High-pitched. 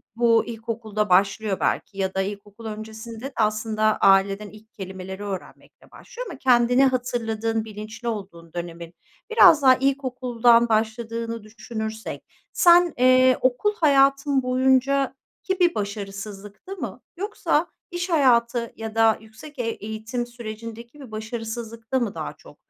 Yes: high, 230 Hz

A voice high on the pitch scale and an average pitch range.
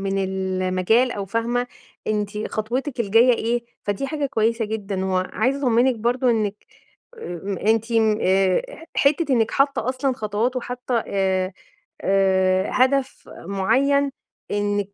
Yes: high, 220 Hz; average, 4.5 semitones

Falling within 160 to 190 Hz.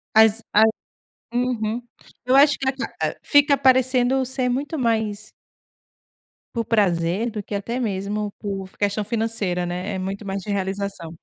No: high, 215 Hz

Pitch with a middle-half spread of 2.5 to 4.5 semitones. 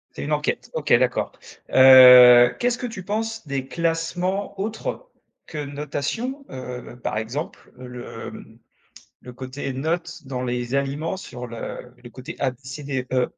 No: average, 4.9 semitones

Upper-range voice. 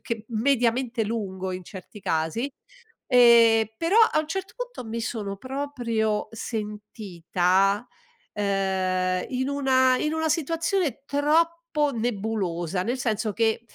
Yes: high, 230 Hz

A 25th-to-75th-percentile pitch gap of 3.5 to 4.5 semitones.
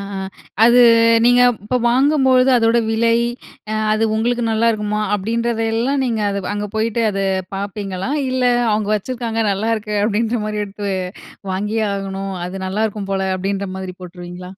No: average, 2.9 semitones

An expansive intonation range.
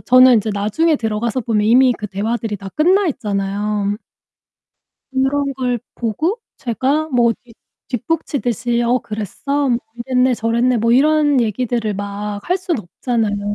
No: average, 3.9 semitones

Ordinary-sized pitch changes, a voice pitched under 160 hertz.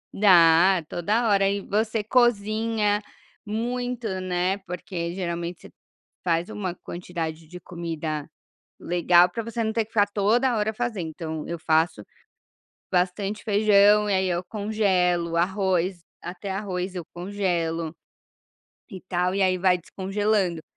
No: average, 3.2 semitones; high, 190 Hz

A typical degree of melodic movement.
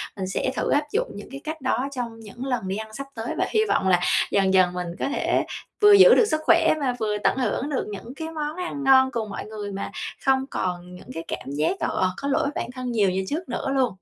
No: wide, 6.1 semitones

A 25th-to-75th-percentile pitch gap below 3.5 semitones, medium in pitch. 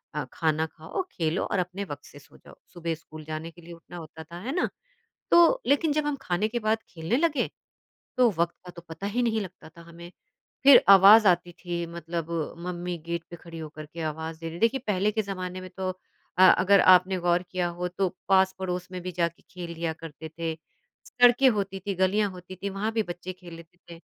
Yes: average, 3.1 semitones; medium, 180 Hz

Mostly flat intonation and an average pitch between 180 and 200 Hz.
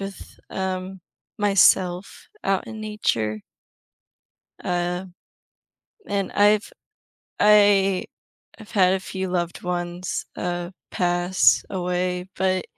Yes: narrow, 1.8 semitones; medium, 185 Hz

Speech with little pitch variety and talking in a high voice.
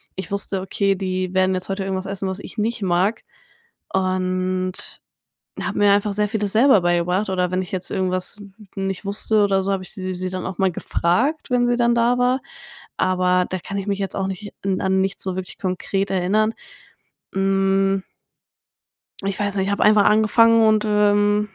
Yes: narrow, 2.0 semitones; high, 195 Hz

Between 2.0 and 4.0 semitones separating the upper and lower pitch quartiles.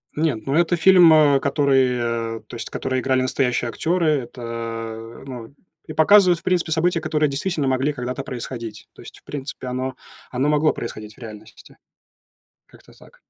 No: average, 4.7 semitones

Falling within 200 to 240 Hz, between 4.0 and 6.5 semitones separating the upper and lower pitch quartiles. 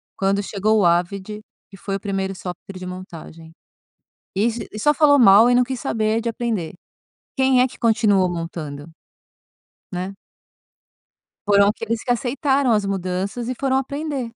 Yes: high, 210 Hz; average, 4.6 semitones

